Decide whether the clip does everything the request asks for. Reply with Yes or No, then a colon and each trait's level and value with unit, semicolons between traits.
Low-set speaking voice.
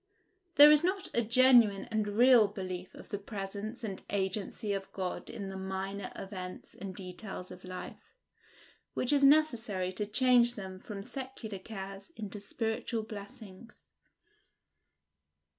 No: high, 205 Hz